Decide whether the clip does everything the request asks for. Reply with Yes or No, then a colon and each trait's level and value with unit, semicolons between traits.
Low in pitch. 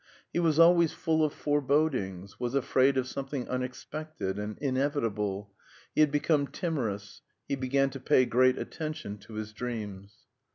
Yes: low, 130 Hz